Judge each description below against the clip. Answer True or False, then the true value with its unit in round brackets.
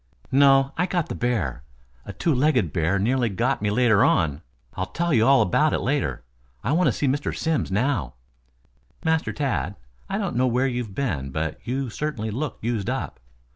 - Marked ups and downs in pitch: True (6.3 semitones)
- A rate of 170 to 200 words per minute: True (190 wpm)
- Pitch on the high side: False (125 Hz)